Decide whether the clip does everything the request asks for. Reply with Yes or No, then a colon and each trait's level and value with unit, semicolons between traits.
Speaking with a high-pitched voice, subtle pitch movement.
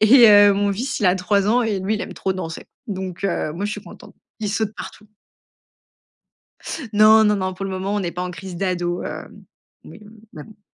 Yes: high, 200 Hz; narrow, 2.2 semitones